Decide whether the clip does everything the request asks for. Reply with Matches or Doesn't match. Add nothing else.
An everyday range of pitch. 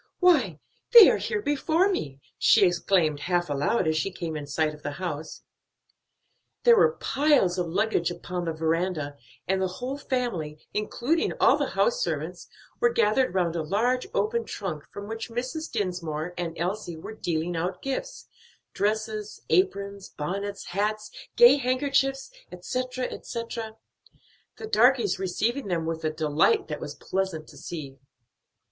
Doesn't match